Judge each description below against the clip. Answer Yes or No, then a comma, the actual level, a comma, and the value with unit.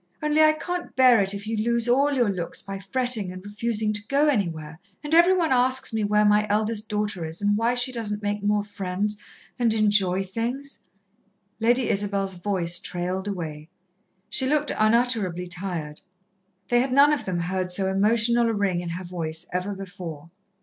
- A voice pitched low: No, high, 205 Hz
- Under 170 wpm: No, average, 185 wpm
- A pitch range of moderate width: Yes, average, 4.4 semitones